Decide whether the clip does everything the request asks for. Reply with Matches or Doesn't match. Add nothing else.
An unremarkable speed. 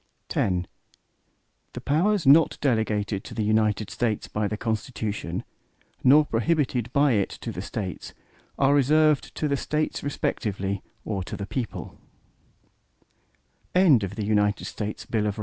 Doesn't match